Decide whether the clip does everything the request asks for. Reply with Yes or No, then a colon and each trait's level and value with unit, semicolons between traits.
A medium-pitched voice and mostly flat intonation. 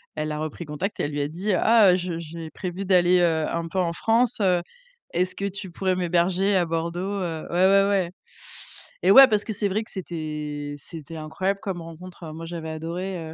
No: medium, 175 Hz; average, 3.0 semitones